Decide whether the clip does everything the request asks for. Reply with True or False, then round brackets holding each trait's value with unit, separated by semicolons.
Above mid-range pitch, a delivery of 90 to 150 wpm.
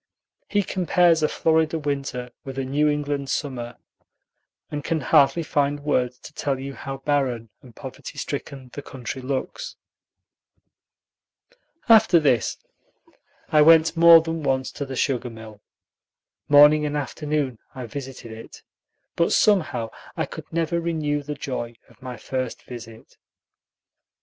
False (140 Hz; 135 wpm)